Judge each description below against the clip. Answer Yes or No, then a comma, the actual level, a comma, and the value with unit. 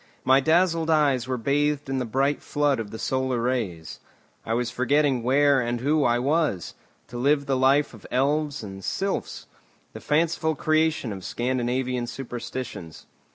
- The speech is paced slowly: No, average, 155 wpm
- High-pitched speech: No, low, 130 Hz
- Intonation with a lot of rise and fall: No, average, 3.4 semitones